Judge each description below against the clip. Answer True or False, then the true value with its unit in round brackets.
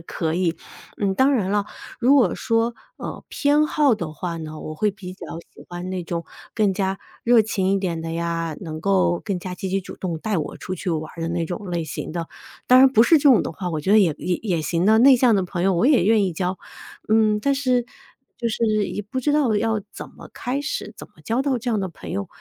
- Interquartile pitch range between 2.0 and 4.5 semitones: False (5.2 semitones)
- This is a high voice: True (195 Hz)